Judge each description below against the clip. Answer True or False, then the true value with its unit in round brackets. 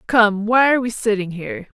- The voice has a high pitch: True (220 Hz)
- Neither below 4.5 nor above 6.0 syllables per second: True (5.8 syllables/s)